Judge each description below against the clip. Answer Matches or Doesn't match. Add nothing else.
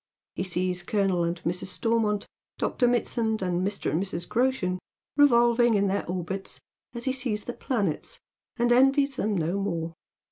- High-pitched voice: Matches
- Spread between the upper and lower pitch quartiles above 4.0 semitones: Matches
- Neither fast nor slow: Matches